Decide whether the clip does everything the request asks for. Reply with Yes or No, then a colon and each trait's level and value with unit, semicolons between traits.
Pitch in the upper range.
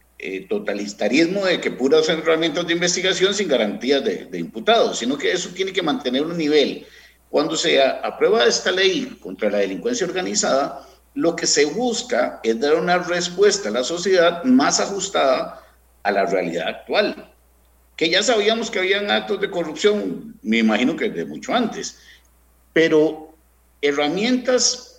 No: medium, 175 Hz